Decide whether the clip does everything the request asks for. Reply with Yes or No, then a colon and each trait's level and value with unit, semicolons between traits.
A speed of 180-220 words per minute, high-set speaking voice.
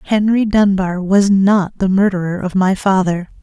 No: average, 160 wpm; high, 195 Hz